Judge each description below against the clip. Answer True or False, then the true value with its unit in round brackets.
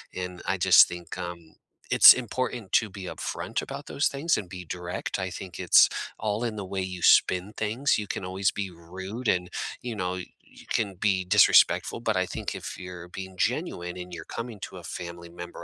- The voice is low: True (95 Hz)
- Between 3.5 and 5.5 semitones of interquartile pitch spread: False (2.8 semitones)